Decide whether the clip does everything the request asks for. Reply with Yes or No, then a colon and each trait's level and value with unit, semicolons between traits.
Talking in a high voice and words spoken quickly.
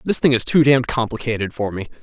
No: low, 120 Hz; fast, 235 wpm